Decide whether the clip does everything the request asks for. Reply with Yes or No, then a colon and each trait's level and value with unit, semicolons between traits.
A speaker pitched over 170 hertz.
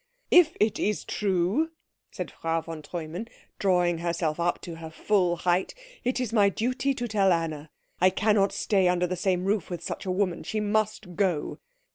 Yes: medium, 185 Hz